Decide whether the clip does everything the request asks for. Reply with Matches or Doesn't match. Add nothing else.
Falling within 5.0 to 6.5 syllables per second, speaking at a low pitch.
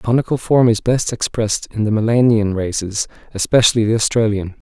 Matches